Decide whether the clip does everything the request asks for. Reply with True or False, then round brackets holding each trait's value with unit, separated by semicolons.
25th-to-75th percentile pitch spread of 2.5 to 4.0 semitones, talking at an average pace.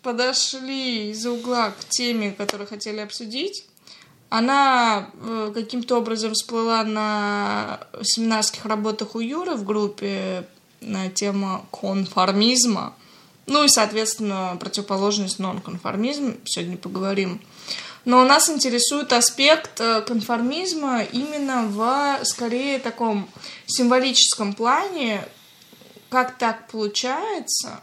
False (3.6 semitones; 95 wpm)